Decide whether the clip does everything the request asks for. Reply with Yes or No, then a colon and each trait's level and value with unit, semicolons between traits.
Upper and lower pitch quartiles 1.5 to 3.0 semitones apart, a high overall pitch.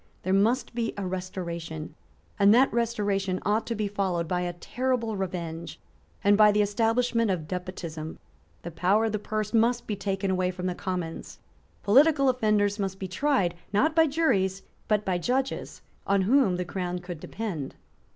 No: average, 3.9 semitones; high, 200 Hz